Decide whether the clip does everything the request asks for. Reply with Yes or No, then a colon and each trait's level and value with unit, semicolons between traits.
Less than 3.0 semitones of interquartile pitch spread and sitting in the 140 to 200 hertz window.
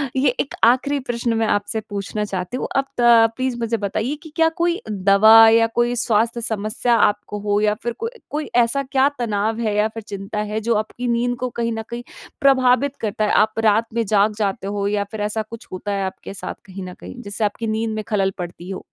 No: narrow, 2.6 semitones; high, 220 Hz